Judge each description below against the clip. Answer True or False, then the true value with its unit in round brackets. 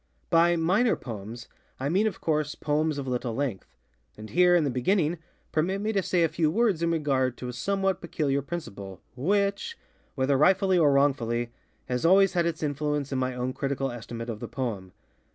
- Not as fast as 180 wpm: False (190 wpm)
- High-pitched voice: False (150 Hz)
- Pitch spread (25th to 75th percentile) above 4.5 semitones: True (5.6 semitones)